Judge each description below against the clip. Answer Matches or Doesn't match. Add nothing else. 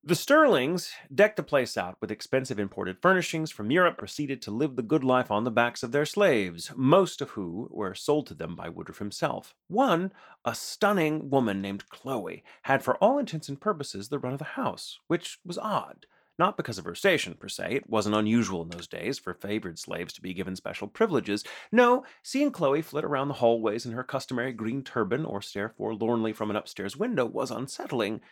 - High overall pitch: Doesn't match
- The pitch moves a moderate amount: Doesn't match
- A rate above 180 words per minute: Matches